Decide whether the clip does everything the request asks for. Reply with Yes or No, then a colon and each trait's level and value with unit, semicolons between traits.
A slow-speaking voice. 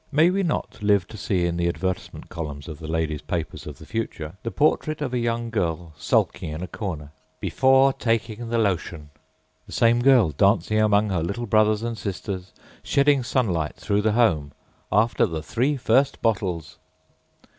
No: average, 165 wpm